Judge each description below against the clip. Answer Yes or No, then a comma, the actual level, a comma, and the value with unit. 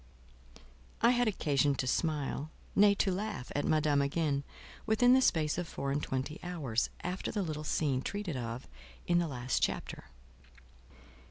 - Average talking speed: Yes, average, 150 wpm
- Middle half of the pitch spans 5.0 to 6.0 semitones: Yes, wide, 5.4 semitones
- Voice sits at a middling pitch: Yes, medium, 155 Hz